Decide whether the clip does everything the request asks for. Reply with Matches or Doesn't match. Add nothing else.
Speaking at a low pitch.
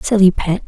Doesn't match